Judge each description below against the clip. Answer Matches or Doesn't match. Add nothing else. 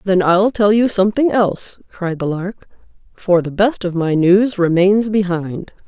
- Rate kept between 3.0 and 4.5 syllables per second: Matches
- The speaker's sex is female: Matches